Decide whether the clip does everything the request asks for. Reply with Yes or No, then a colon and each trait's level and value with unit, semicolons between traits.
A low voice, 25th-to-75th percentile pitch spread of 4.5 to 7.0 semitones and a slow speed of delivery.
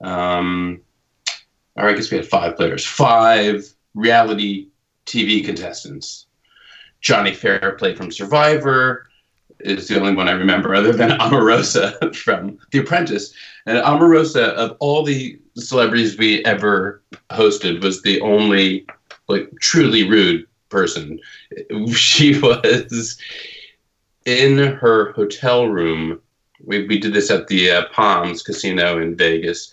Yes: low, 115 Hz; wide, 5.6 semitones; slow, 125 wpm